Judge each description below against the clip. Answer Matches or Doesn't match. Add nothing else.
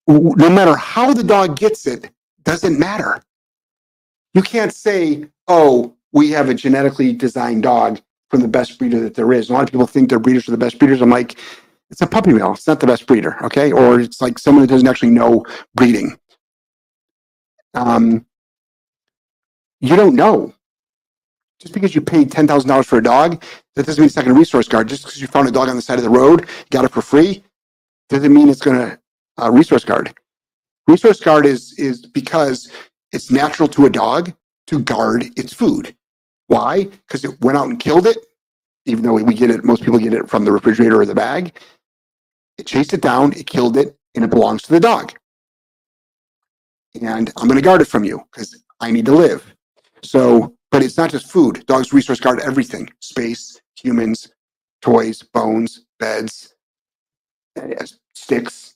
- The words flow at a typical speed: Matches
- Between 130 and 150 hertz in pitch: Matches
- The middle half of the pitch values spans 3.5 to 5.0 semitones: Matches